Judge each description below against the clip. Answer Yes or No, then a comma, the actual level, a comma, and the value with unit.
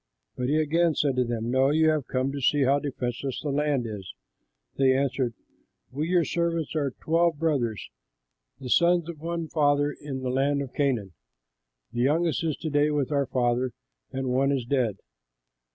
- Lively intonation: No, average, 3.3 semitones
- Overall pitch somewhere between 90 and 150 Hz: Yes, medium, 140 Hz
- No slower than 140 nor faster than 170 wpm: No, average, 180 wpm